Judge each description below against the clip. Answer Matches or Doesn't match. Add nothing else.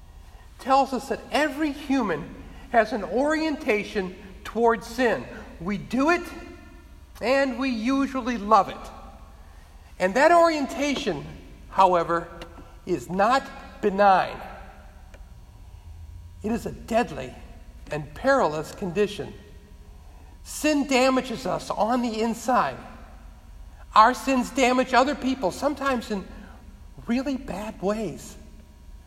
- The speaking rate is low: Matches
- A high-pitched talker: Matches